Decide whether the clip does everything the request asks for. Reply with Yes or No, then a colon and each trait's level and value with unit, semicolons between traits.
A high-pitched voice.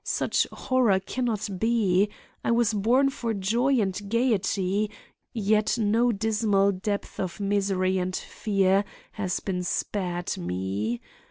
Yes: high, 200 Hz